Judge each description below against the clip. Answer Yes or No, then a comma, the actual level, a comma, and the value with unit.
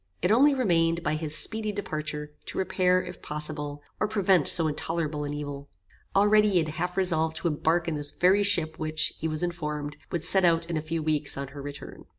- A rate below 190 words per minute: No, fast, 205 wpm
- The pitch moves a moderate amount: Yes, average, 3.3 semitones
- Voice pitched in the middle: Yes, medium, 165 Hz